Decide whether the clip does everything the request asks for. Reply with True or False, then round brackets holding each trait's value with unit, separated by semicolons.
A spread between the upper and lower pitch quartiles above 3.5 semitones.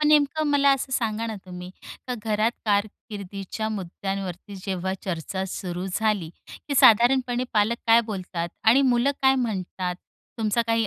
True (4.2 semitones)